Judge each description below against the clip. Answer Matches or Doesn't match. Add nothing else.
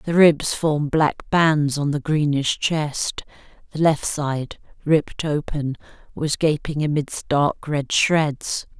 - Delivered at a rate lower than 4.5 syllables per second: Matches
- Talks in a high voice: Doesn't match